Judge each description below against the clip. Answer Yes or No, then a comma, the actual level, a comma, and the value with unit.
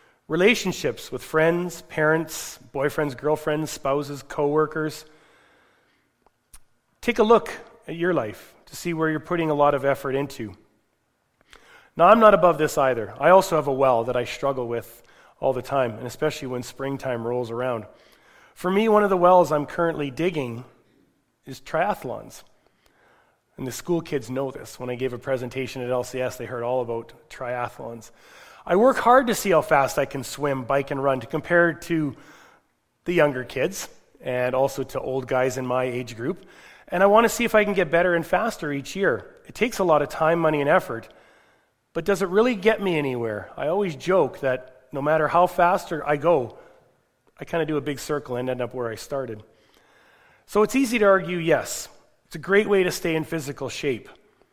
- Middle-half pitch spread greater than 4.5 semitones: Yes, average, 5.1 semitones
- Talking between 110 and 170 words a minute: No, average, 190 wpm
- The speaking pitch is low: No, medium, 145 Hz